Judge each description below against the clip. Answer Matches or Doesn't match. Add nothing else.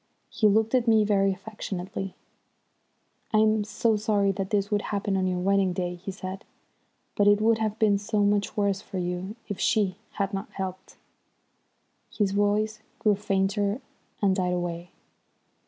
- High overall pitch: Matches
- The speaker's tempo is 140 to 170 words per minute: Matches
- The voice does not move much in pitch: Matches